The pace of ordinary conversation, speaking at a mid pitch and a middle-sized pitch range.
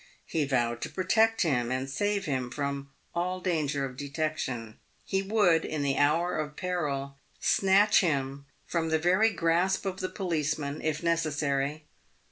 Yes: average, 150 wpm; medium, 155 Hz; average, 4.6 semitones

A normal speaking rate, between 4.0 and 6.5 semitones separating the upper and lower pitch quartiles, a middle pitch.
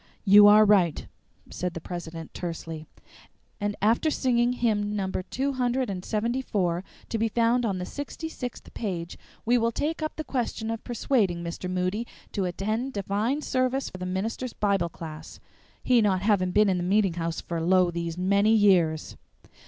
No: average, 170 wpm; average, 4.7 semitones; high, 205 Hz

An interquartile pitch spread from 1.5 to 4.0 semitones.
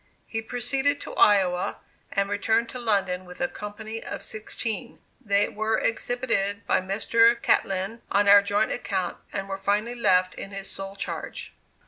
Yes: average, 2.7 semitones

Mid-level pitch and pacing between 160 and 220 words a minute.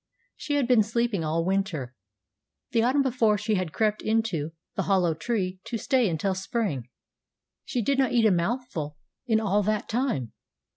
No: high, 215 Hz; average, 165 wpm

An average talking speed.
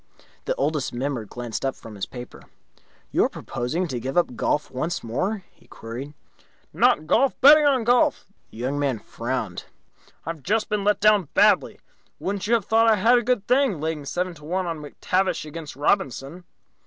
Yes: average, 180 wpm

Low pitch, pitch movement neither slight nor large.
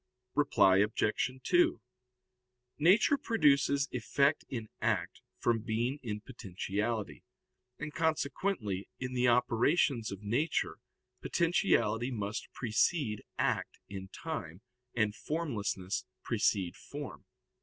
No: low, 120 Hz; wide, 5.9 semitones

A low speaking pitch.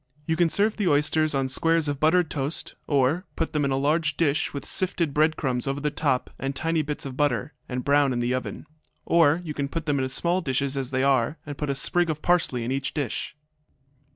No: medium, 145 Hz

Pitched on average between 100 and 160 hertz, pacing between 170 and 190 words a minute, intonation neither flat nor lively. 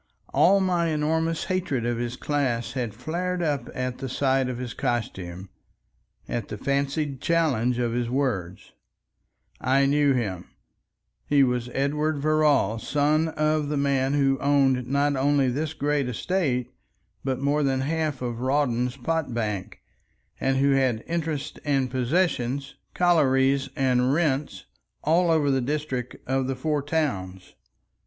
No: low, 135 Hz; average, 140 wpm; average, 3.2 semitones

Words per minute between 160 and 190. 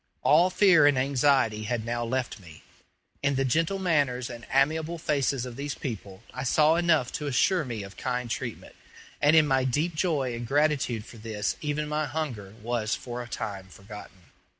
Yes: average, 180 wpm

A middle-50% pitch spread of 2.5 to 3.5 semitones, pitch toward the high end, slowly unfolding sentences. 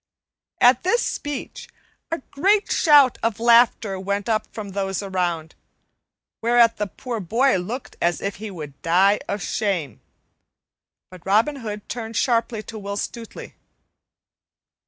No: average, 3.9 semitones; high, 215 Hz; slow, 130 wpm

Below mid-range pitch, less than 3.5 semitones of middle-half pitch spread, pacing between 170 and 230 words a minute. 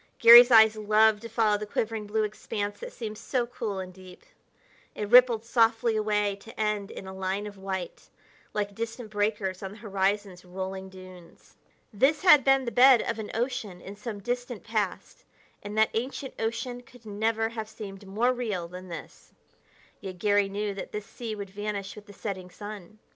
No: high, 210 Hz; narrow, 2.5 semitones; average, 180 wpm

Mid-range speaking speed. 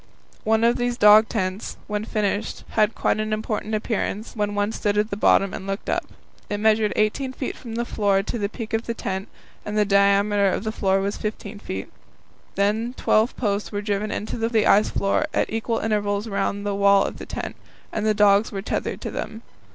No: fast, 215 wpm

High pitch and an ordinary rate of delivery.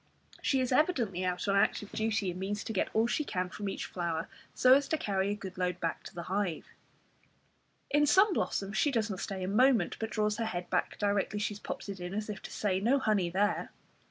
No: high, 205 Hz; fast, 235 wpm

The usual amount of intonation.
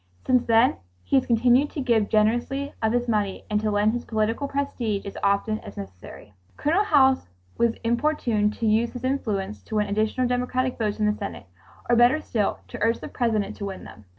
Yes: average, 3.1 semitones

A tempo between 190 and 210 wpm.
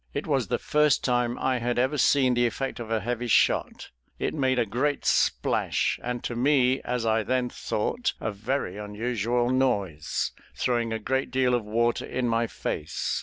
No: average, 180 wpm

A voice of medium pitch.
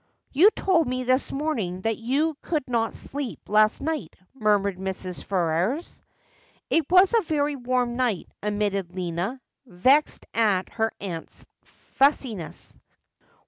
No: high, 235 Hz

